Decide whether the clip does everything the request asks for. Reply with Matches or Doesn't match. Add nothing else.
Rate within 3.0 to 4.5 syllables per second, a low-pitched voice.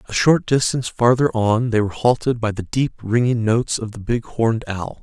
Doesn't match